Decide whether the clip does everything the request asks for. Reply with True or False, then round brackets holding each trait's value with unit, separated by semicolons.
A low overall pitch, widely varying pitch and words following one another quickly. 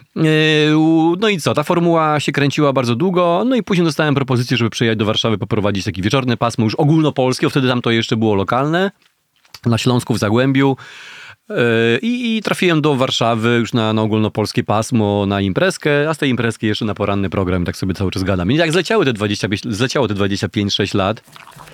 True (125 Hz; 6.1 semitones; 180 wpm)